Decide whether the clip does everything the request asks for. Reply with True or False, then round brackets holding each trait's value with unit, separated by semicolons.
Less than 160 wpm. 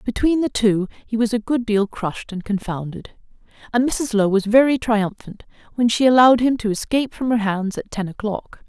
False (200 wpm)